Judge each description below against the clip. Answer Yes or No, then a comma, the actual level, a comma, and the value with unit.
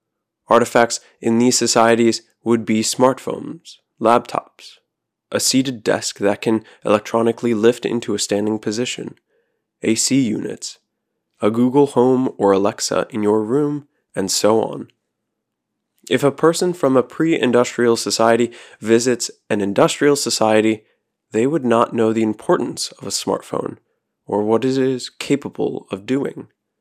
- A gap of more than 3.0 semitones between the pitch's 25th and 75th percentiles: No, average, 2.7 semitones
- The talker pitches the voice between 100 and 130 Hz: Yes, low, 115 Hz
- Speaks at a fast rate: No, slow, 135 wpm